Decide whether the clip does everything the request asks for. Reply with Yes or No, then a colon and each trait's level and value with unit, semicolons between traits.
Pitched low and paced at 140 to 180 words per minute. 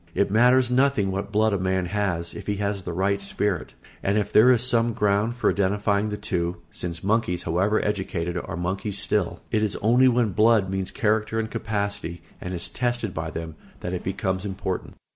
No: low, 100 Hz; average, 195 wpm